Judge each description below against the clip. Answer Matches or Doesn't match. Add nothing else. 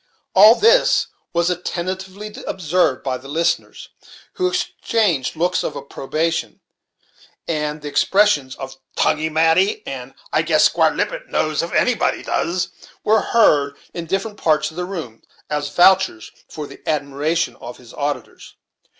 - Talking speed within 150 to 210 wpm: Doesn't match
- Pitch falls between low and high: Matches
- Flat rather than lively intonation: Doesn't match